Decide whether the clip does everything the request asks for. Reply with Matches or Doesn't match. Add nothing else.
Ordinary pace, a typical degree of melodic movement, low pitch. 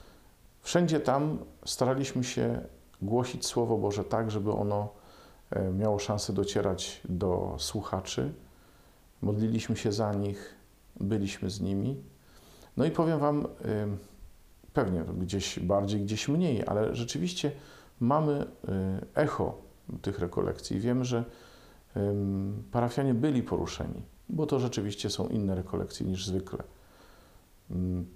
Doesn't match